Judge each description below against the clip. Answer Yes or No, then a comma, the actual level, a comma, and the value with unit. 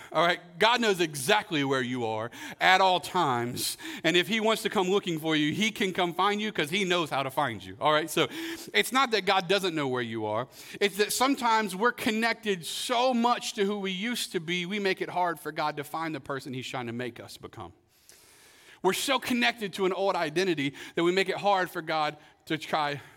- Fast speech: Yes, fast, 230 wpm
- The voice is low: No, medium, 185 Hz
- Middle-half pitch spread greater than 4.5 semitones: Yes, wide, 5.6 semitones